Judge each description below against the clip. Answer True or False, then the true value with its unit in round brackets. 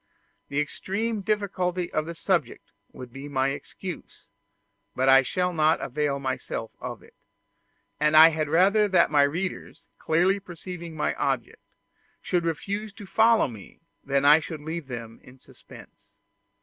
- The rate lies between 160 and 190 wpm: False (150 wpm)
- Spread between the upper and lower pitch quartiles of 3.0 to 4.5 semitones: False (5.0 semitones)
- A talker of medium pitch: True (160 Hz)